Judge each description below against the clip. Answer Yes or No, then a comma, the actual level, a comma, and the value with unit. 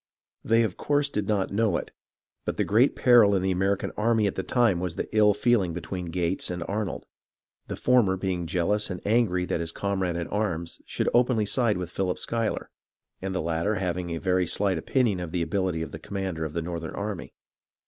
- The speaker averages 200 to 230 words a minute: Yes, fast, 205 wpm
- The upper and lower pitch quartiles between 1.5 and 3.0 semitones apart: No, average, 3.4 semitones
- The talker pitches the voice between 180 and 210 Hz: No, very low, 95 Hz